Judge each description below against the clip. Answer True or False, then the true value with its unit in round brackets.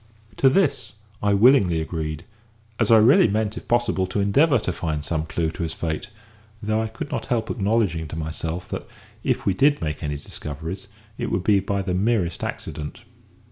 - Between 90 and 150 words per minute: False (185 wpm)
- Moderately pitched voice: False (95 Hz)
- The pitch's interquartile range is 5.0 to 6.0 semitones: True (5.6 semitones)